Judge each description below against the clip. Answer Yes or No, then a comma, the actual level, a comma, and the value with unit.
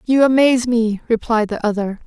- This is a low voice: No, high, 230 Hz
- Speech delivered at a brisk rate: No, average, 175 wpm